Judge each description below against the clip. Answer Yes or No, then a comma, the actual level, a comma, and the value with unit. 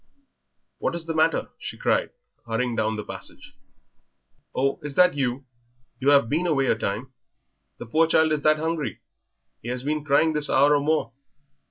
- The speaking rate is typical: Yes, average, 175 wpm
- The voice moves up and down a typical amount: Yes, average, 3.9 semitones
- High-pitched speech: No, medium, 145 Hz